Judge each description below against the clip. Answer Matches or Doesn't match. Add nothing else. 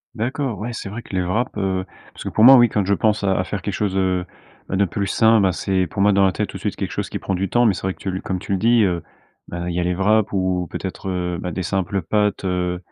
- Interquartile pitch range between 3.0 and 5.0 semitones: Doesn't match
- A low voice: Matches